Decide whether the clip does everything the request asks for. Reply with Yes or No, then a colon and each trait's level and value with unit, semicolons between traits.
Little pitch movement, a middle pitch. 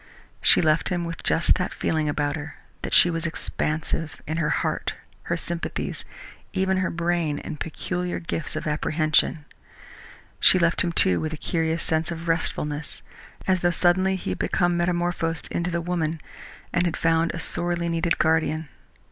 Yes: narrow, 1.6 semitones; medium, 165 Hz